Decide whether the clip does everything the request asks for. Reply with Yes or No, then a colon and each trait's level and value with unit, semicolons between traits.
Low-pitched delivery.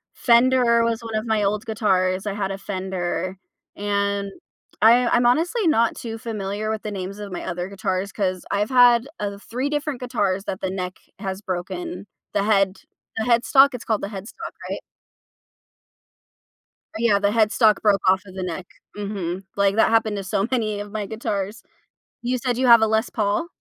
No: high, 210 Hz